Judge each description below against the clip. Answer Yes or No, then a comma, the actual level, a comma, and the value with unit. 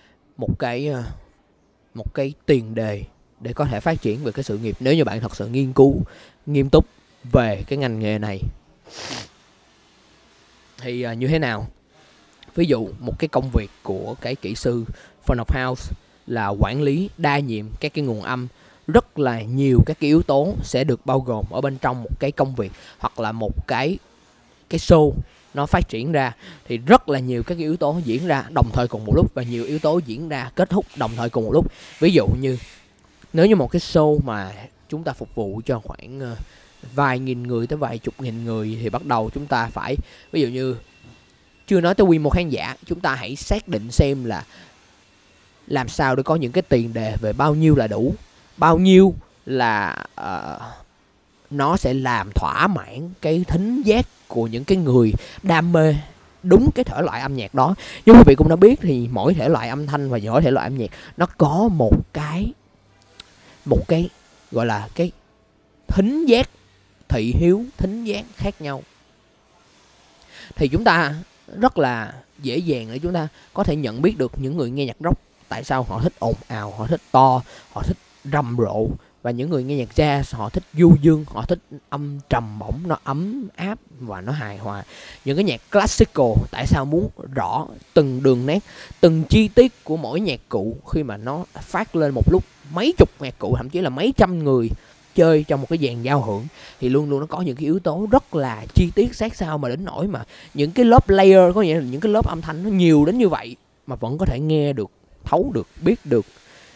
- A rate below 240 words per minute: Yes, average, 210 wpm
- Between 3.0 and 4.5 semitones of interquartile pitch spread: No, wide, 5.6 semitones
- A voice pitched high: No, medium, 140 Hz